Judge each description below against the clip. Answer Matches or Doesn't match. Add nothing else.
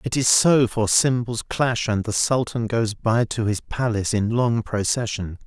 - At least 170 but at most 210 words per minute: Matches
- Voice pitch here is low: Matches